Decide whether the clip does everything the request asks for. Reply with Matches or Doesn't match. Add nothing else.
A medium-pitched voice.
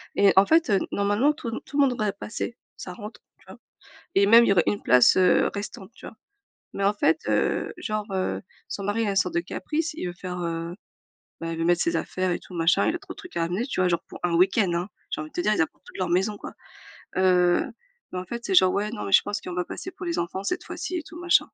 Doesn't match